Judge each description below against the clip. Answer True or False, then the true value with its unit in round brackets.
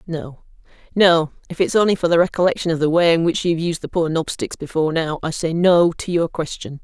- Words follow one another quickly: True (230 wpm)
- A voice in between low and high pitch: True (165 Hz)